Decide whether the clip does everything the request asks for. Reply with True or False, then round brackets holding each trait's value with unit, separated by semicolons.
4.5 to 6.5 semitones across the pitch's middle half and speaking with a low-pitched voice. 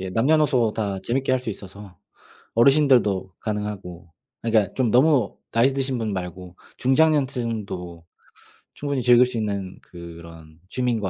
True (5.3 semitones; 110 Hz)